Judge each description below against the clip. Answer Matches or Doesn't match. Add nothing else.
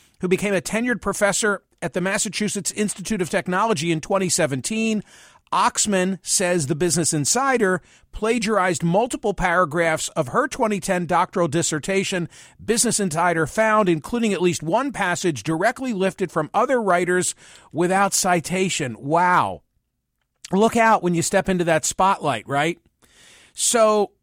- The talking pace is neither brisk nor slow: Doesn't match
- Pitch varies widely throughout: Doesn't match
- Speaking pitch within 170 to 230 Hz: Matches